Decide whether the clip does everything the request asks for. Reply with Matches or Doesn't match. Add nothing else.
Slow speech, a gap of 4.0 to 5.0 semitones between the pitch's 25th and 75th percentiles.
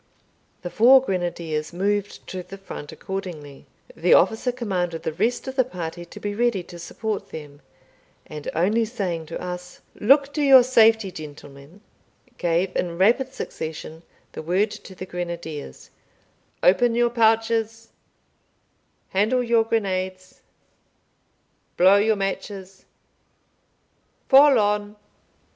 Matches